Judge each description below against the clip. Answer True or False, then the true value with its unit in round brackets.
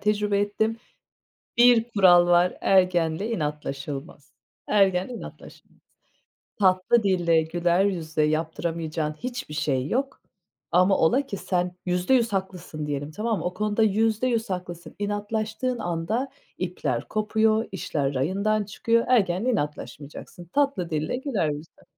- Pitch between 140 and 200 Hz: True (190 Hz)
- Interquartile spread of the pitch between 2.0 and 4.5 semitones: False (4.9 semitones)